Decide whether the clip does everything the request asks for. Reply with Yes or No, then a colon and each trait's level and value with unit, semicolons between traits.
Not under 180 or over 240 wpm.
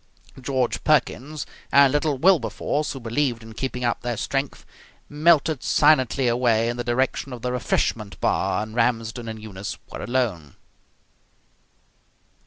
No: slow, 135 wpm